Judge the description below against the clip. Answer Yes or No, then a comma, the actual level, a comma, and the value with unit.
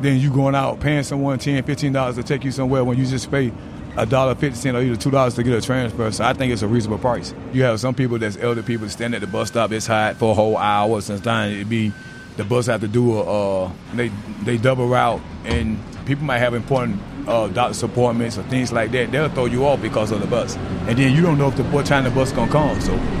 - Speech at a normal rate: No, fast, 260 wpm